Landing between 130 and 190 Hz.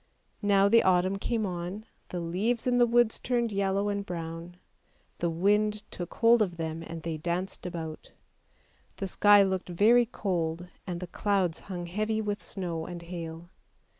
Yes: medium, 185 Hz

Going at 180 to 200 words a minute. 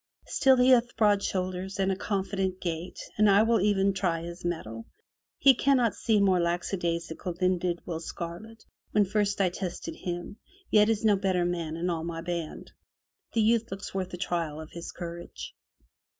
Yes: average, 190 wpm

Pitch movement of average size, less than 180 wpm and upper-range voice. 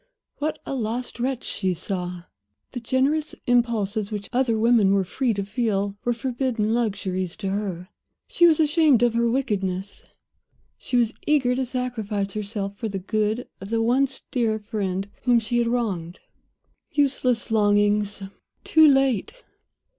Yes: average, 3.9 semitones; average, 145 wpm; high, 225 Hz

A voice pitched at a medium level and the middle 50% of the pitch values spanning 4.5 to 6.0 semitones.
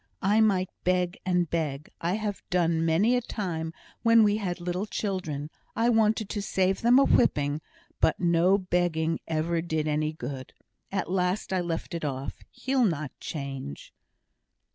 No: medium, 175 Hz; average, 4.0 semitones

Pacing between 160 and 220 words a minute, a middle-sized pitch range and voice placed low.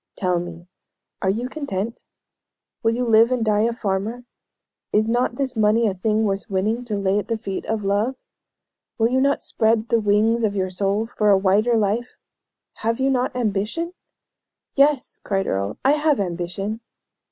No: average, 175 wpm; average, 3.4 semitones; high, 220 Hz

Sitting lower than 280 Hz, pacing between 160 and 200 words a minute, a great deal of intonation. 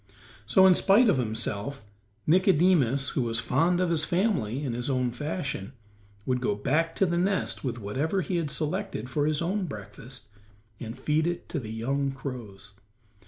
Yes: medium, 140 Hz; average, 170 wpm; wide, 6.2 semitones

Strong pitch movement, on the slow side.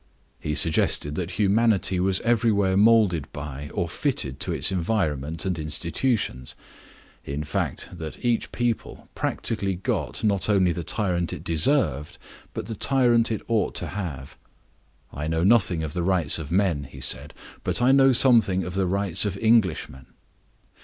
No: wide, 5.9 semitones; average, 155 wpm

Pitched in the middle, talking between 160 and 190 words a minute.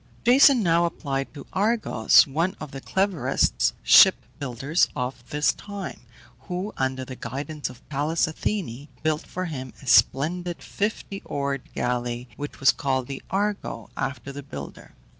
No: medium, 145 Hz; average, 145 wpm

